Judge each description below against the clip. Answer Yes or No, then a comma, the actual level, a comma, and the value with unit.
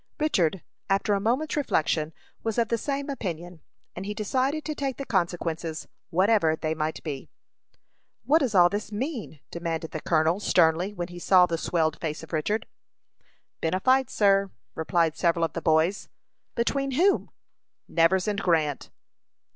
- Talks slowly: No, average, 160 wpm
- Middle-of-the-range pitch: Yes, medium, 180 Hz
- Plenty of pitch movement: Yes, wide, 5.8 semitones